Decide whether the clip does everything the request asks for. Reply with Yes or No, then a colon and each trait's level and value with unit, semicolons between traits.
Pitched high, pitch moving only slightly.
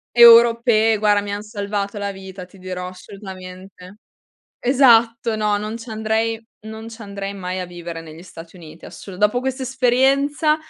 No: high, 210 Hz; average, 3.6 semitones